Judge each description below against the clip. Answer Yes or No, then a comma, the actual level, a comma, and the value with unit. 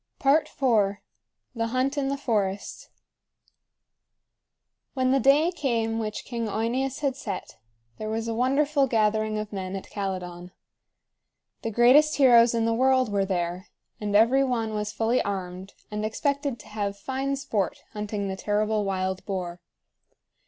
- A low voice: No, high, 225 Hz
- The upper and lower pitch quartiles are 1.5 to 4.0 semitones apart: No, average, 4.5 semitones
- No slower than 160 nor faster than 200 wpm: No, average, 145 wpm